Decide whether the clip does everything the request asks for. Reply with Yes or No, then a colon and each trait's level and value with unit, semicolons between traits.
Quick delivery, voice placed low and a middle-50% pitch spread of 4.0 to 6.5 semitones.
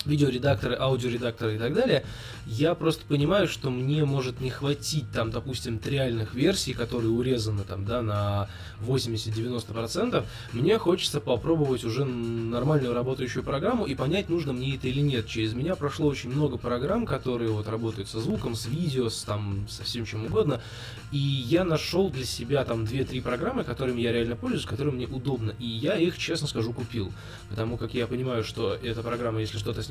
No: fast, 175 wpm; low, 125 Hz; average, 3.6 semitones